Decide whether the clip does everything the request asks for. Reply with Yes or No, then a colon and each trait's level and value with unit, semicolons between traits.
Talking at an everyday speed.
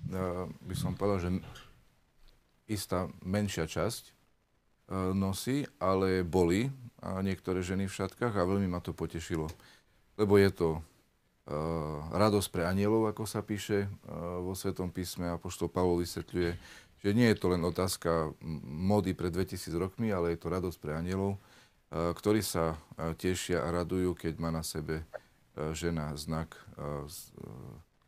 Yes: average, 150 wpm